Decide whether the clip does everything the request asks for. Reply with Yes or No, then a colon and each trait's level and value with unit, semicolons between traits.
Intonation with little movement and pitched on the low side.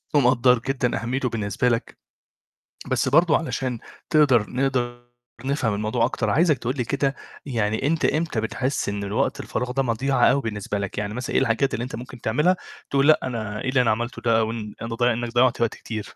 No: average, 3.1 semitones; low, 120 Hz